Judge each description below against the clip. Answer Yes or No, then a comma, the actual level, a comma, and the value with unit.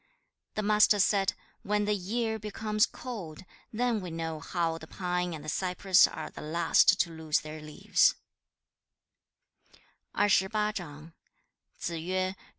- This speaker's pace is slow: Yes, slow, 115 wpm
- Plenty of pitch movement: No, average, 4.4 semitones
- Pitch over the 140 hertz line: Yes, medium, 185 Hz